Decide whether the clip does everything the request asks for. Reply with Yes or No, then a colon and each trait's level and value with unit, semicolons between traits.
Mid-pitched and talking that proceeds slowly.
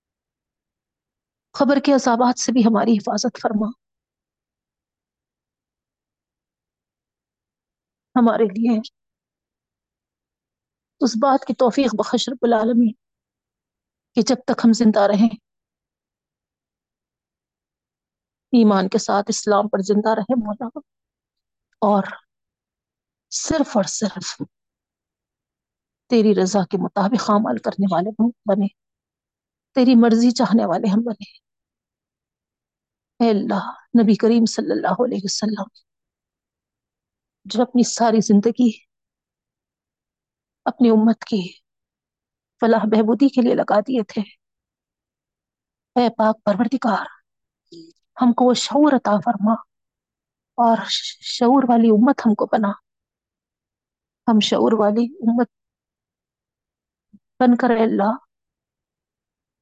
No: high, 230 Hz; slow, 95 wpm